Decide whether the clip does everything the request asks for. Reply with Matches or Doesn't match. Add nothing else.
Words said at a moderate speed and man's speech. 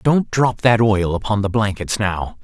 Matches